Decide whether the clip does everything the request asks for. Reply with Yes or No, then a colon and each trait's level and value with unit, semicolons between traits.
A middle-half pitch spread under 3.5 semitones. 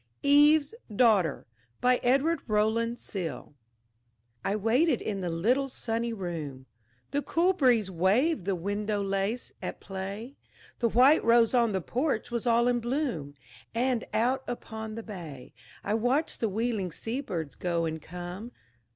No: average, 4.7 semitones